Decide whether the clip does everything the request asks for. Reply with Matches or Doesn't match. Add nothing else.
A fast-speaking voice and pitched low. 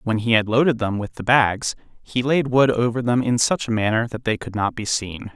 Matches